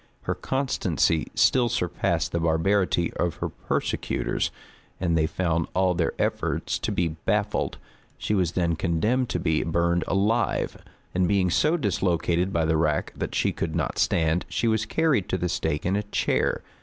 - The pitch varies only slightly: No, average, 3.7 semitones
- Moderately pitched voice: No, very low, 90 Hz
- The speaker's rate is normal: Yes, average, 170 wpm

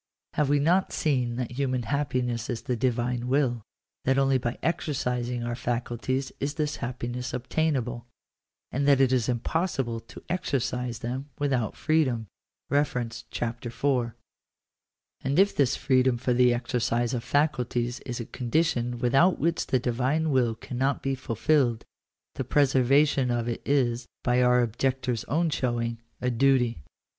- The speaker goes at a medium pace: Yes, average, 150 wpm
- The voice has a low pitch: Yes, low, 125 Hz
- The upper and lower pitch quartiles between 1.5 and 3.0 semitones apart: Yes, narrow, 2.5 semitones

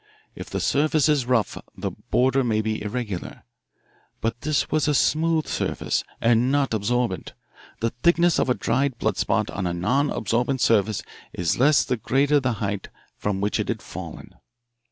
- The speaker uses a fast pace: No, average, 170 wpm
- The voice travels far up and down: No, average, 4.6 semitones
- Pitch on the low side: Yes, low, 125 Hz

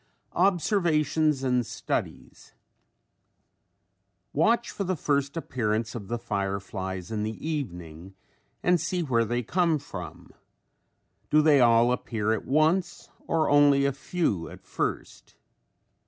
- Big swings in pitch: Yes, wide, 6.5 semitones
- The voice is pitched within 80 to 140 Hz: Yes, low, 135 Hz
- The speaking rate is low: Yes, slow, 120 wpm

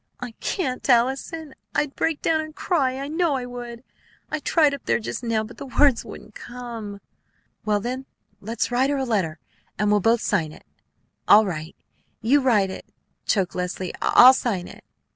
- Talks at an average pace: Yes, average, 180 wpm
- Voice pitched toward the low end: No, high, 240 Hz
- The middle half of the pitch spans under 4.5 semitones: No, average, 4.8 semitones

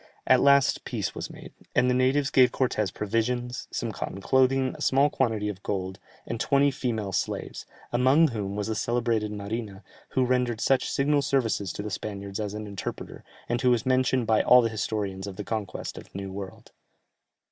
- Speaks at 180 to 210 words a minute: Yes, average, 190 wpm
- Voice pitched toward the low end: Yes, low, 115 Hz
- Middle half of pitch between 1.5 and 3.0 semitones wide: No, average, 3.9 semitones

